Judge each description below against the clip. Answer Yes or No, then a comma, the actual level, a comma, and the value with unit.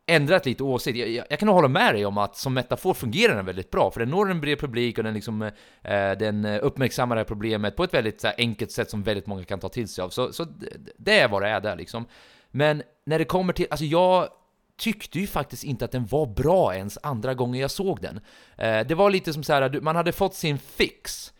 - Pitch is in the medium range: No, low, 130 Hz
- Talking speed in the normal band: No, fast, 250 wpm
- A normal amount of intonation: No, wide, 6.5 semitones